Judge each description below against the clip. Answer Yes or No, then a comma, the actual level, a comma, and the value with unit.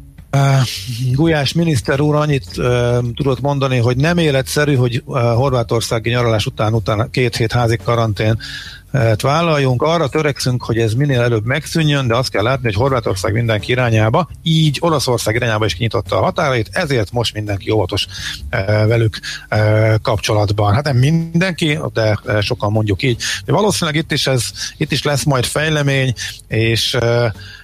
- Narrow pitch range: No, average, 4.4 semitones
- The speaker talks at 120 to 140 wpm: No, fast, 155 wpm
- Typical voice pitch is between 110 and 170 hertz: Yes, low, 120 Hz